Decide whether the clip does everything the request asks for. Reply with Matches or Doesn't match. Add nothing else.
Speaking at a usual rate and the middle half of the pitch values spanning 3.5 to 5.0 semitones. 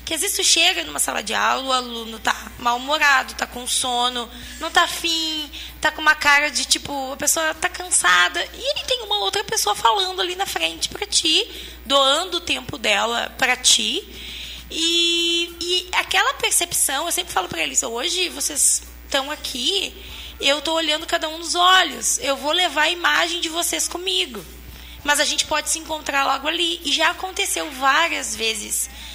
Matches